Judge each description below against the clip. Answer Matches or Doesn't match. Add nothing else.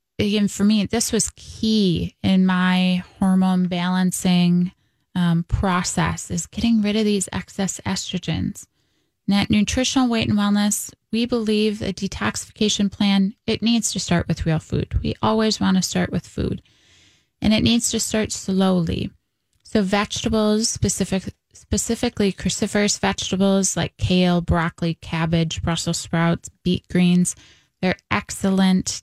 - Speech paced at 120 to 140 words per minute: Matches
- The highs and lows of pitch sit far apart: Doesn't match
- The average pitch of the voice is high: Matches